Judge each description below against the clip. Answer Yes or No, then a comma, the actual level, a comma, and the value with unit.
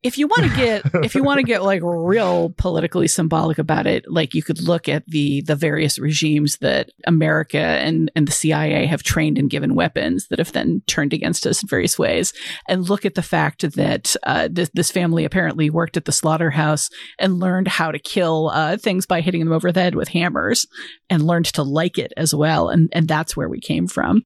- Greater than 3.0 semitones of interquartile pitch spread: No, average, 2.7 semitones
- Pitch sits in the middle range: Yes, medium, 165 Hz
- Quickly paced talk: Yes, fast, 220 wpm